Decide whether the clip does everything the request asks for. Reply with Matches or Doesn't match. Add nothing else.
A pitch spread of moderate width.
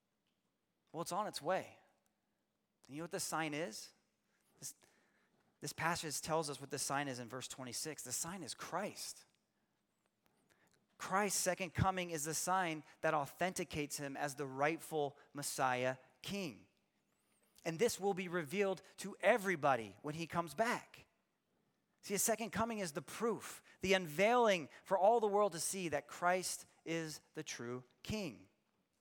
Matches